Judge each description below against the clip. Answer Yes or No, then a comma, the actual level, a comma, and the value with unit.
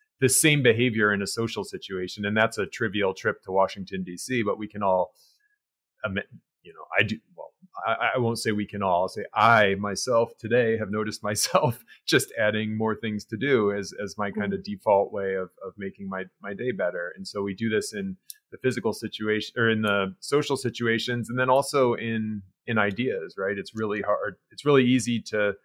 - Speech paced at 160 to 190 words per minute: No, fast, 205 wpm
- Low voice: Yes, low, 110 Hz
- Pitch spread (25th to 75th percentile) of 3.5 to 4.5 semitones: Yes, average, 3.8 semitones